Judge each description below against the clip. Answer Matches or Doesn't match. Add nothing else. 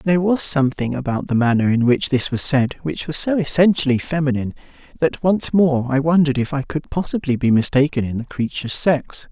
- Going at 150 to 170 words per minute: Doesn't match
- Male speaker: Matches